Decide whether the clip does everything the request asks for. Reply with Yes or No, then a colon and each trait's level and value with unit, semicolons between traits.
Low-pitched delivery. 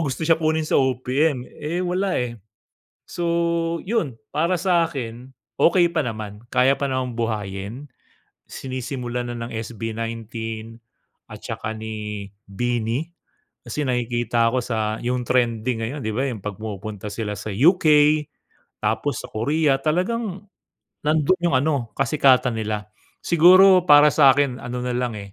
Yes: low, 125 Hz